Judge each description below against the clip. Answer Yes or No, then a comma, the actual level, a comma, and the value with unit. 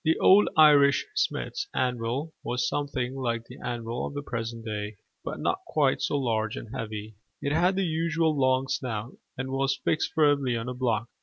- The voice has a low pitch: Yes, low, 130 Hz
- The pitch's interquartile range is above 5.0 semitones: No, average, 3.8 semitones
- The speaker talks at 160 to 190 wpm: Yes, average, 180 wpm